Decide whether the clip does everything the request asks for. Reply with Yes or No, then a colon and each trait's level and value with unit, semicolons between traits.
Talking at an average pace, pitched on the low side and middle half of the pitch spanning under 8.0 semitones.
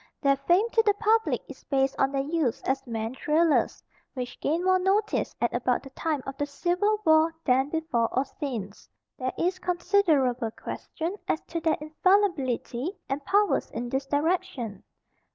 No: average, 165 wpm; very high, 300 Hz; wide, 5.6 semitones